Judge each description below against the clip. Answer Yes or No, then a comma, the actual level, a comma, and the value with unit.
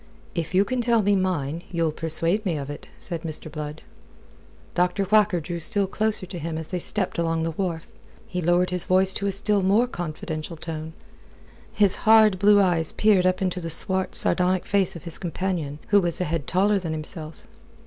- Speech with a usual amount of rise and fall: Yes, average, 3.2 semitones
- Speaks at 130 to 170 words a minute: No, average, 195 wpm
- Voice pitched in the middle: Yes, medium, 180 Hz